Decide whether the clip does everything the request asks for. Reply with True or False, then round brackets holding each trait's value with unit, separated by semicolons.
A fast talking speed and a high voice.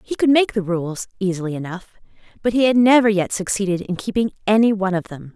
True (215 wpm; 200 Hz)